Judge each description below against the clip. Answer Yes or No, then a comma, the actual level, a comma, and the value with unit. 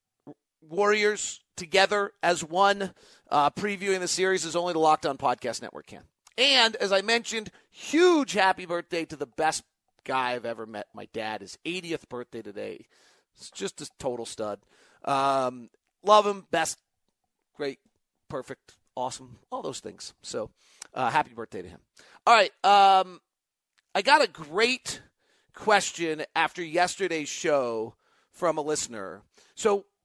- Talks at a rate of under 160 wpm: Yes, average, 140 wpm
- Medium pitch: Yes, medium, 175 Hz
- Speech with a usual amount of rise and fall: No, wide, 5.7 semitones